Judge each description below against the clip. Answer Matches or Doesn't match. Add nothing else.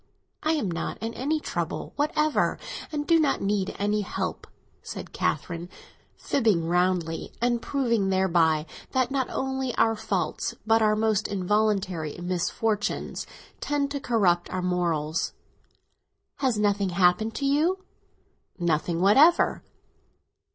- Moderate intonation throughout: Doesn't match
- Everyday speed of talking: Doesn't match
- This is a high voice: Matches